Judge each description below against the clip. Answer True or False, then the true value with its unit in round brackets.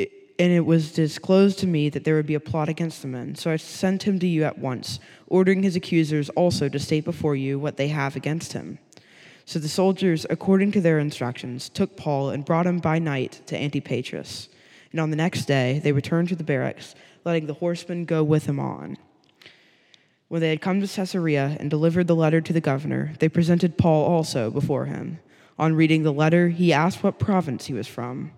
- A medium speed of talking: False (210 wpm)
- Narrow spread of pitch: False (3.3 semitones)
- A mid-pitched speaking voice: True (160 Hz)